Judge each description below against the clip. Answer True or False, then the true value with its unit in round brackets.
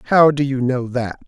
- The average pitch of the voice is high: False (130 Hz)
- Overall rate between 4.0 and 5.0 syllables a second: True (4.9 syllables/s)